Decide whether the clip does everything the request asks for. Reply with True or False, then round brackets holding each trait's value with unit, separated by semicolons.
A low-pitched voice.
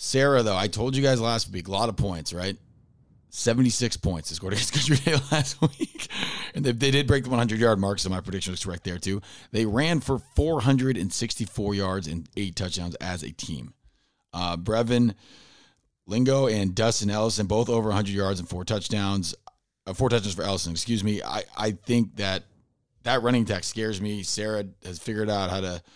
True (105 Hz)